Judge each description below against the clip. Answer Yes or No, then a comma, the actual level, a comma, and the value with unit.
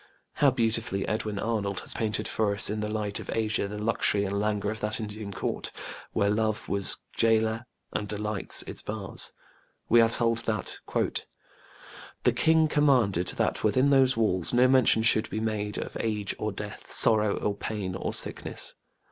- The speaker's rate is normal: Yes, average, 170 wpm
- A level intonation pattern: Yes, narrow, 1.7 semitones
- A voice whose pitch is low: Yes, low, 110 Hz